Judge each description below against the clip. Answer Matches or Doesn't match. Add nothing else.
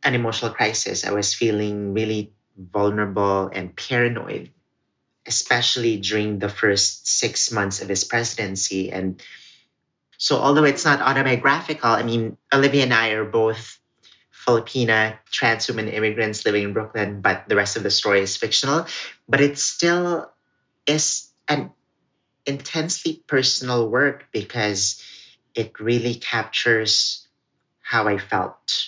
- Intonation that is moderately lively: Matches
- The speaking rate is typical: Doesn't match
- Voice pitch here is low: Matches